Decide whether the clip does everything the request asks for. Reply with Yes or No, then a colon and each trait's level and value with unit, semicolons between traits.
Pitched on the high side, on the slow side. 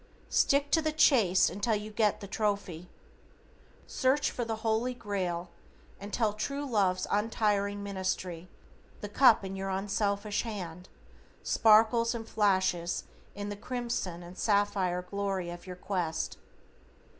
Yes: high, 205 Hz; slow, 130 wpm